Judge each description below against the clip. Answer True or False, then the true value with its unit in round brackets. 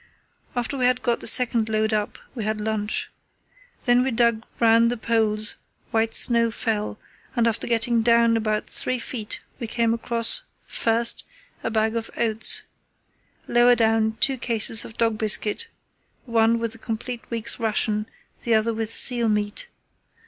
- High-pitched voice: True (230 Hz)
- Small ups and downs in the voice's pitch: True (1.3 semitones)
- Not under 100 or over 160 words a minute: True (155 wpm)